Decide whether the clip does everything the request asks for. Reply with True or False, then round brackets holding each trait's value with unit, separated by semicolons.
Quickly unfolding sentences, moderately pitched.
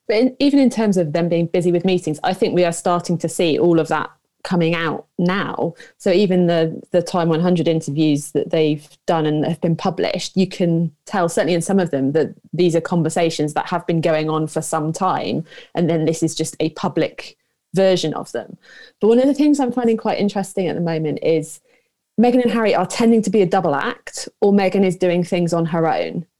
True (225 wpm; 175 Hz)